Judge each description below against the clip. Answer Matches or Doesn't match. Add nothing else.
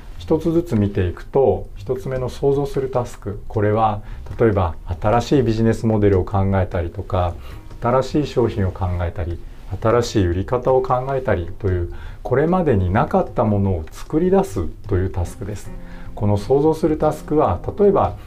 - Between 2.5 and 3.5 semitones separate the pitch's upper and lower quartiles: Doesn't match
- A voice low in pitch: Matches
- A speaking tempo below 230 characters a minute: Doesn't match